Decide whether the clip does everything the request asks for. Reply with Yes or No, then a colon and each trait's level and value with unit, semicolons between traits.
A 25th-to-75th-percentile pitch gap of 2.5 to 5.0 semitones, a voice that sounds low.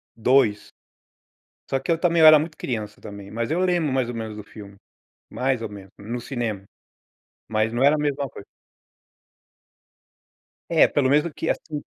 No: wide, 5.5 semitones; low, 130 Hz